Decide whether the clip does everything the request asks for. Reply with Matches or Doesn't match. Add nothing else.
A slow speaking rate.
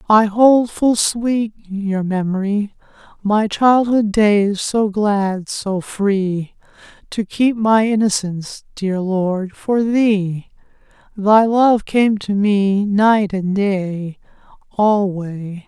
Matches